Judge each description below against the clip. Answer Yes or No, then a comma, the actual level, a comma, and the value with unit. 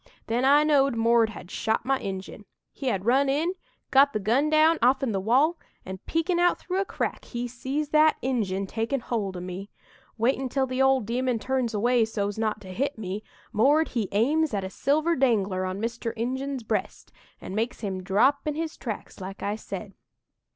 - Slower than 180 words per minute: No, average, 195 wpm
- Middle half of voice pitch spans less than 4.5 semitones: No, average, 4.9 semitones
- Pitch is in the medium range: No, high, 240 Hz